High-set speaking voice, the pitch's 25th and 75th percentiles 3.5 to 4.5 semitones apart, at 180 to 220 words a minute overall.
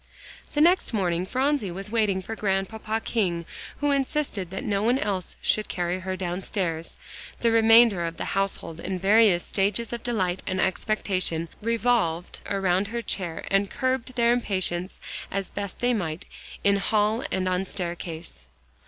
No: high, 195 Hz; average, 3.9 semitones; average, 150 wpm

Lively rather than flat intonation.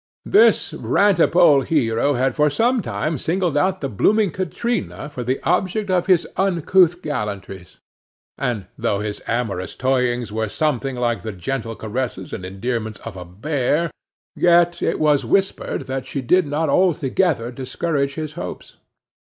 Yes: wide, 6.9 semitones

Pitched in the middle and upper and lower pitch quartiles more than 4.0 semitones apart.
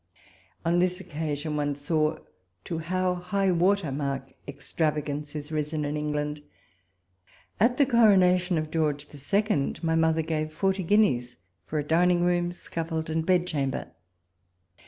No: medium, 160 Hz; average, 3.3 semitones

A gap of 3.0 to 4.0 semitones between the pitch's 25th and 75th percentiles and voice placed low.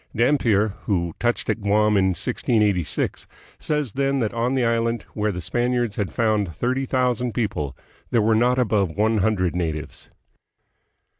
Yes: average, 3.5 semitones; low, 110 Hz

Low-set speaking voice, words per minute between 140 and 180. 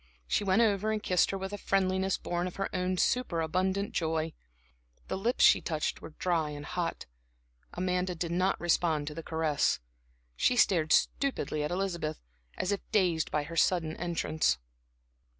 No: medium, 175 Hz; average, 170 wpm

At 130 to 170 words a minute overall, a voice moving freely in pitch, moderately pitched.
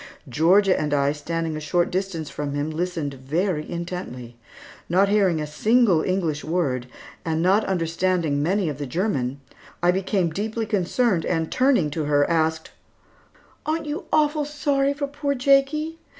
Yes: average, 150 wpm; wide, 5.8 semitones; medium, 175 Hz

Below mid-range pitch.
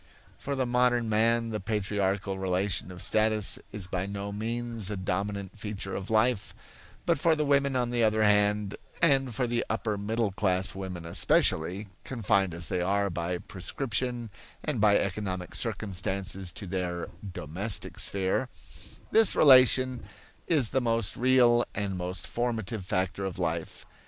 Yes: low, 105 Hz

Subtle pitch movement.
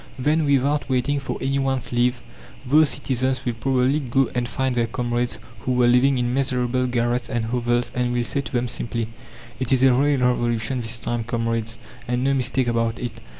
Yes: narrow, 1.9 semitones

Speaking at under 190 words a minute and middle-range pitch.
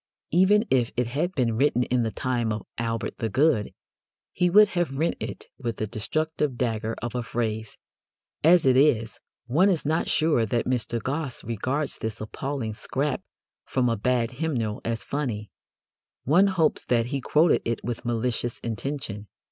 No: average, 165 wpm; low, 125 Hz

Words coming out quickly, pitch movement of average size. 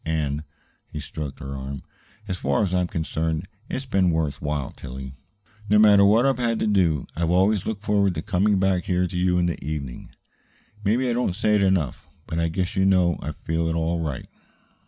Yes: fast, 210 wpm; average, 4.2 semitones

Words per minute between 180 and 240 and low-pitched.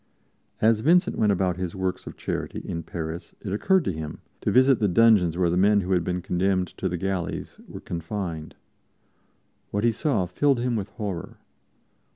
Yes: average, 185 wpm; very low, 95 Hz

